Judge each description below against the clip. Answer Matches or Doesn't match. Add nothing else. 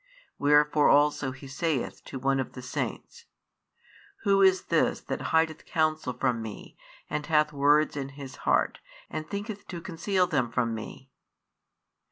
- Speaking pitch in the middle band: Matches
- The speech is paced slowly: Doesn't match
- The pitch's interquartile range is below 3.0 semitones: Doesn't match